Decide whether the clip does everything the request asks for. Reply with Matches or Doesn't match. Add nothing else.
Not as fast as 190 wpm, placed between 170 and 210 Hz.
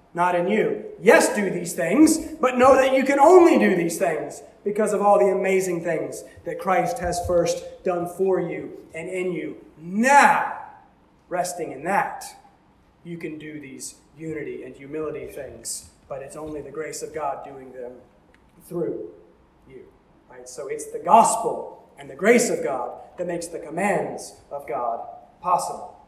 Matches